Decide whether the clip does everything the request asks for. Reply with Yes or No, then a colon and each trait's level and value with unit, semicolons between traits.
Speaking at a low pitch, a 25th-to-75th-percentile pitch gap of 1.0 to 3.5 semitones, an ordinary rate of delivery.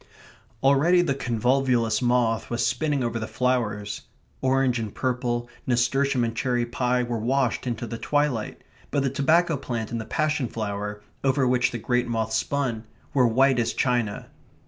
Yes: low, 125 Hz; average, 2.7 semitones; average, 160 wpm